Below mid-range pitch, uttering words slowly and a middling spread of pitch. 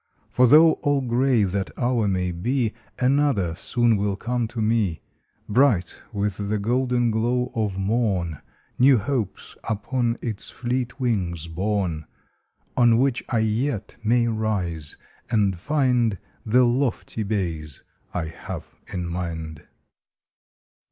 Yes: low, 110 Hz; slow, 125 wpm; average, 4.4 semitones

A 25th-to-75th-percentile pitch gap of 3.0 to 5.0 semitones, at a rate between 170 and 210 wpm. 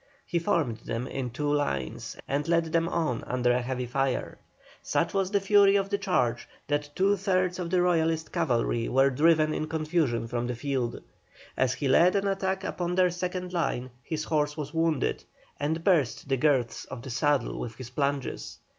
No: wide, 5.6 semitones; average, 185 wpm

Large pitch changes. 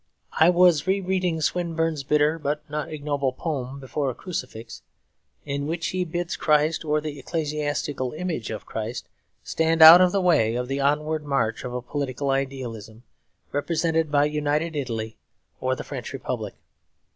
No: average, 3.8 semitones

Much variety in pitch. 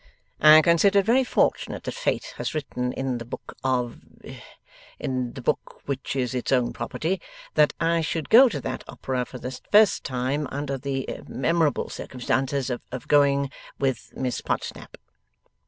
No: average, 3.9 semitones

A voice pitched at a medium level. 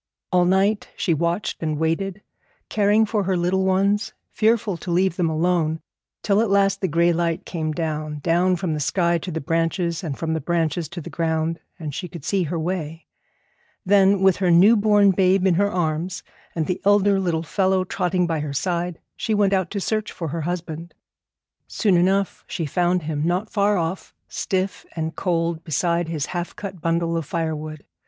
Yes: medium, 175 Hz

